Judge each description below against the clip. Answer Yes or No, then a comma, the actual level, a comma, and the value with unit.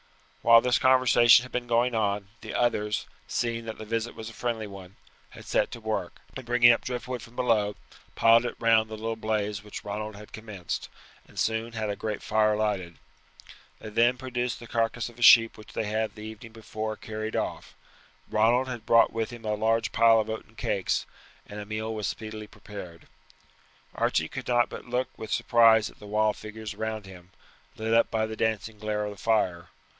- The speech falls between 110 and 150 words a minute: No, average, 200 wpm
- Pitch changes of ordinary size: No, narrow, 1.6 semitones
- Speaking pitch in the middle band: No, low, 110 Hz